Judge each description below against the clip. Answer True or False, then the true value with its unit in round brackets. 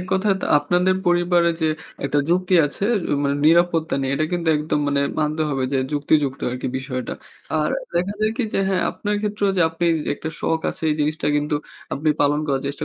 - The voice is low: False (160 Hz)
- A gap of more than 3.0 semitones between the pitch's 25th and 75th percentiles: True (3.5 semitones)